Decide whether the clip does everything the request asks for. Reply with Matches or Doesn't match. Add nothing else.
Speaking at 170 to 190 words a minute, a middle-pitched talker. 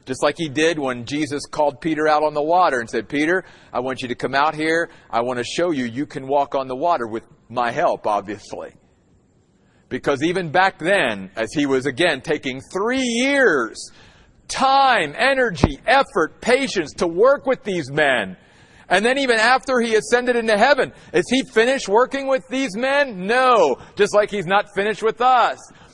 Matches